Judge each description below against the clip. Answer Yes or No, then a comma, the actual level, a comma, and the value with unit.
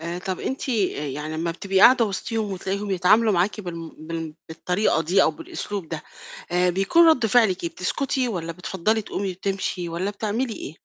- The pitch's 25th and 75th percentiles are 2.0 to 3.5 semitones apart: No, average, 4.2 semitones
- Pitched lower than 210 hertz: Yes, high, 190 Hz